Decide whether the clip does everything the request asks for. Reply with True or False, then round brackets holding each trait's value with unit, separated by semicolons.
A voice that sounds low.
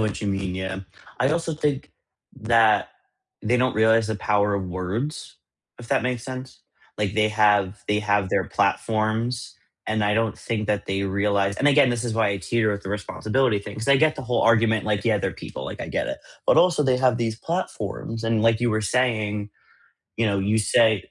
True (110 Hz)